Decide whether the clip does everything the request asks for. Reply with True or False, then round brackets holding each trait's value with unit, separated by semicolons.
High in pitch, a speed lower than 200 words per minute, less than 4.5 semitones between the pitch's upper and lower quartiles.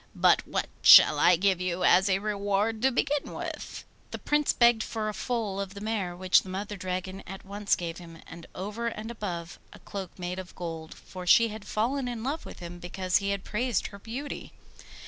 False (200 Hz; 205 wpm; 3.4 semitones)